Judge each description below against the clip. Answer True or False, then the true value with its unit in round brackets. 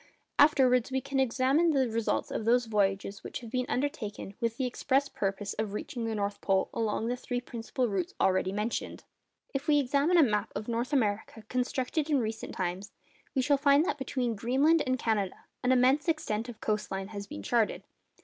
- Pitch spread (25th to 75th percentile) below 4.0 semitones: False (4.3 semitones)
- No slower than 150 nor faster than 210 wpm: True (190 wpm)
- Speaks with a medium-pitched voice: False (240 Hz)